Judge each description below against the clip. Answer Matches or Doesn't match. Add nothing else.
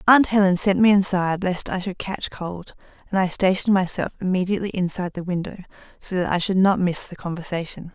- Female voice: Matches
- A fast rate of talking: Doesn't match